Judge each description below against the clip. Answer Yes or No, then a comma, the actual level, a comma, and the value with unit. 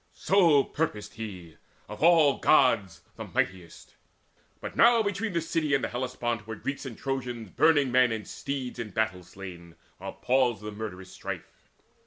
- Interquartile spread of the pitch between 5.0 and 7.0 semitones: Yes, wide, 5.6 semitones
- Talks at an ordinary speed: Yes, average, 150 wpm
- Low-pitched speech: Yes, low, 120 Hz